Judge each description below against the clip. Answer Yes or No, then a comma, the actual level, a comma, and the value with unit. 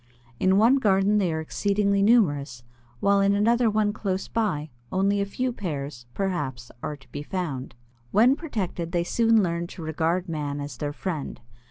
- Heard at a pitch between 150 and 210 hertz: Yes, medium, 185 Hz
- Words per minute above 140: Yes, average, 170 wpm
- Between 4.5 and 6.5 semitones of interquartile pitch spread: Yes, wide, 5.4 semitones